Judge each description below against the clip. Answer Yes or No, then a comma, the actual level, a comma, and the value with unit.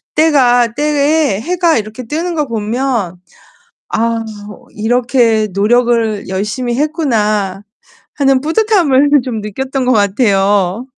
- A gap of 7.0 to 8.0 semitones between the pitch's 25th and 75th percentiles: No, average, 5.1 semitones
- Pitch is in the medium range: No, high, 240 Hz